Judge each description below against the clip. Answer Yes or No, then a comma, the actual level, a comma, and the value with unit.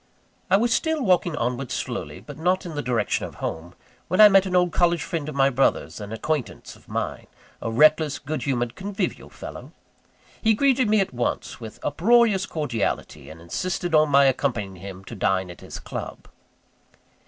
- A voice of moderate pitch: Yes, medium, 150 Hz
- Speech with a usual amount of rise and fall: No, wide, 7.5 semitones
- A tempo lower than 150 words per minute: No, average, 185 wpm